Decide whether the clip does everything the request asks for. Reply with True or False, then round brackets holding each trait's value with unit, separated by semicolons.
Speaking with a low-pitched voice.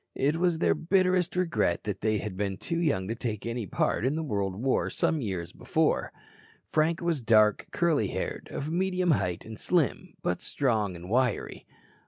True (125 Hz)